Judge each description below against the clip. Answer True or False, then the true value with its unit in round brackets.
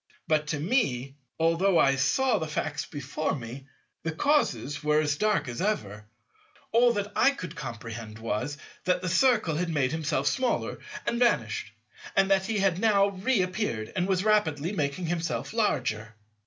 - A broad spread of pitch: True (6.3 semitones)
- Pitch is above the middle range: False (165 Hz)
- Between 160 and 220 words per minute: True (165 wpm)